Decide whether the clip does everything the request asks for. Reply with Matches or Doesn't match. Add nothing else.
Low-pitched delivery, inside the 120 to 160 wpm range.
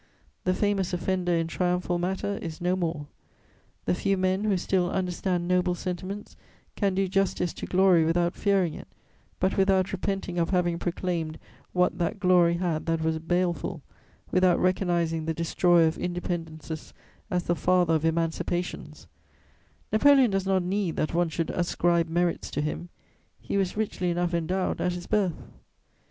Doesn't match